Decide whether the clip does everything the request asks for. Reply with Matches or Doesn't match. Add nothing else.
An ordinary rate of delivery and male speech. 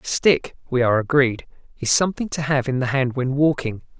Doesn't match